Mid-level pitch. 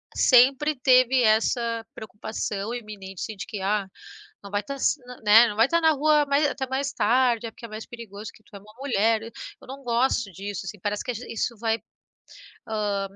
No: high, 225 Hz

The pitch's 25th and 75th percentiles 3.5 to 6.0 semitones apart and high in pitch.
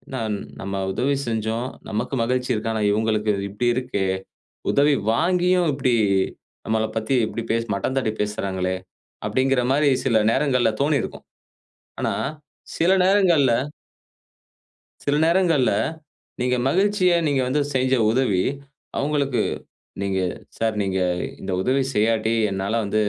No: average, 4.6 semitones; low, 125 Hz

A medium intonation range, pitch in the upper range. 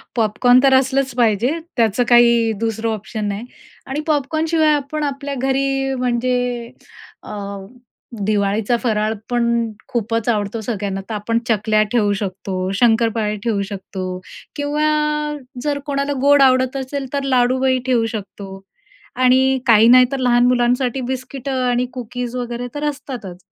Yes: average, 3.4 semitones; high, 245 Hz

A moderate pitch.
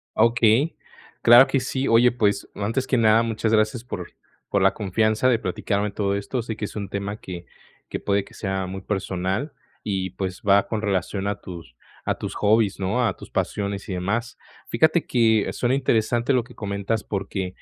No: low, 105 Hz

